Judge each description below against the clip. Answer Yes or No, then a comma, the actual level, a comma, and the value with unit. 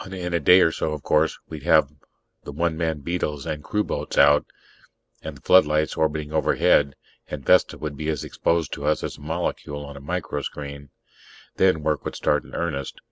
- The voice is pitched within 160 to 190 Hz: No, very low, 75 Hz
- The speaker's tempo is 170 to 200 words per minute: Yes, average, 190 wpm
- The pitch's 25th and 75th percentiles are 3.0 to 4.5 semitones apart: No, narrow, 2.5 semitones